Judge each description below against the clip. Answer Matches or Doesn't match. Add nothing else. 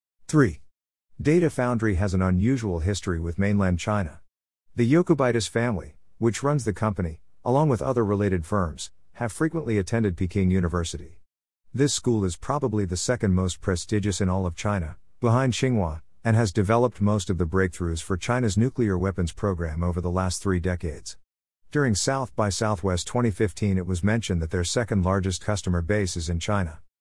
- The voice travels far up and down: Doesn't match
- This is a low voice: Matches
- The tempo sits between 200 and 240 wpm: Doesn't match